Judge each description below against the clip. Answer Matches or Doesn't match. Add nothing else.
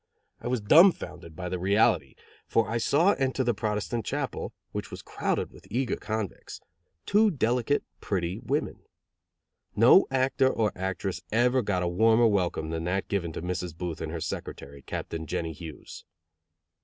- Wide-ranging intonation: Matches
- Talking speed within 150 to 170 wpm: Matches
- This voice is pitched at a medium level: Doesn't match